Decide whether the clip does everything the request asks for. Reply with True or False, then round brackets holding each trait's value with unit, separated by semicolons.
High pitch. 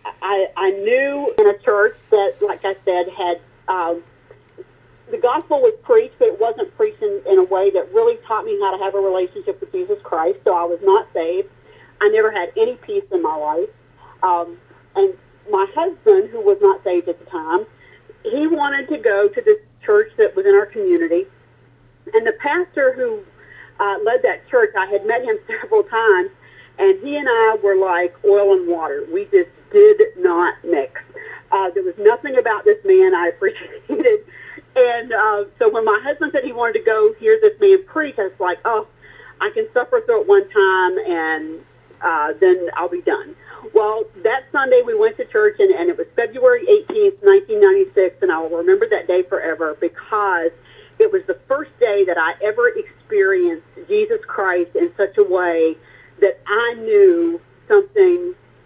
True (390 Hz)